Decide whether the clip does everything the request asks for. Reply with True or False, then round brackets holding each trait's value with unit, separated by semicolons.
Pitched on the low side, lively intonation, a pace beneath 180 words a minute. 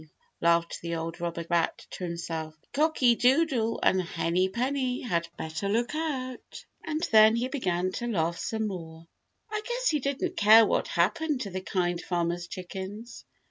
False (200 Hz; 6.9 semitones; 160 wpm)